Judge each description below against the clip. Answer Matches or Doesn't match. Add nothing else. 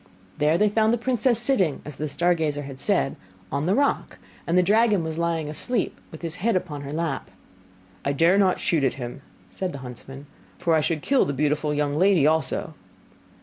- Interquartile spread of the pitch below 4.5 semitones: Doesn't match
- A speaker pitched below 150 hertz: Doesn't match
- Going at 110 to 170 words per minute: Doesn't match